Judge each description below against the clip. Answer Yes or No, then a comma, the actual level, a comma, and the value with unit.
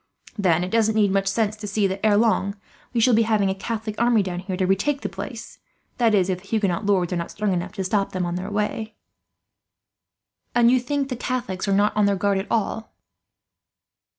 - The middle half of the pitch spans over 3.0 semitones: No, average, 2.7 semitones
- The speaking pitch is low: No, high, 205 Hz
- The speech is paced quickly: Yes, fast, 220 wpm